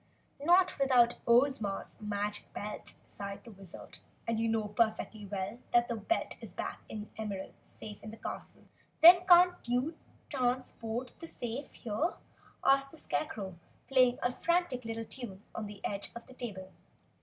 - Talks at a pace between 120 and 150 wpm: No, average, 160 wpm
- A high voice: Yes, high, 235 Hz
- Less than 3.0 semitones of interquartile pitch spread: No, average, 4.3 semitones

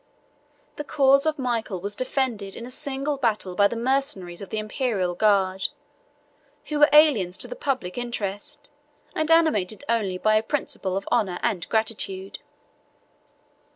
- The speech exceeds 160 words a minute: No, average, 150 wpm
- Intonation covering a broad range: Yes, wide, 6.0 semitones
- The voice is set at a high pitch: Yes, high, 220 Hz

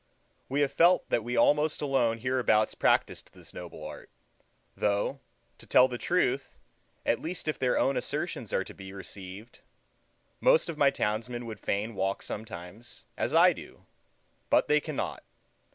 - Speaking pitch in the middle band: No, low, 120 Hz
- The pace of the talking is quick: No, average, 155 wpm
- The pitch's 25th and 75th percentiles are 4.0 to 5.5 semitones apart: Yes, average, 5.2 semitones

